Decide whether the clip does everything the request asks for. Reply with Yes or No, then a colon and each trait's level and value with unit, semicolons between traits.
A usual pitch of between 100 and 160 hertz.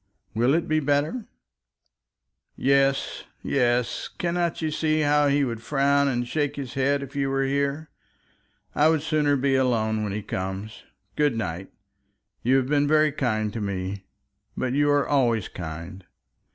Yes: low, 135 Hz